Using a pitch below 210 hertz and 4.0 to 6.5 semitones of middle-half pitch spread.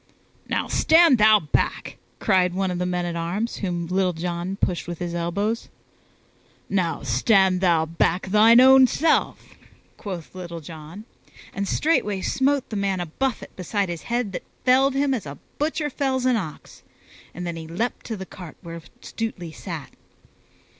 Yes: high, 190 Hz; average, 5.1 semitones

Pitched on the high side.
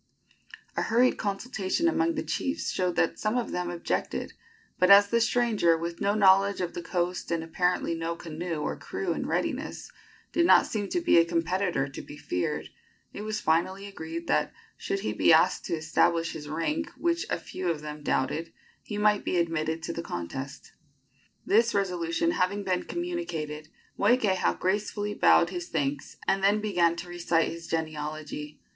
No: medium, 180 Hz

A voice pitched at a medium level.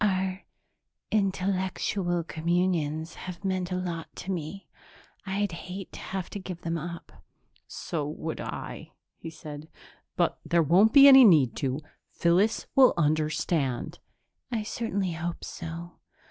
Yes: medium, 175 Hz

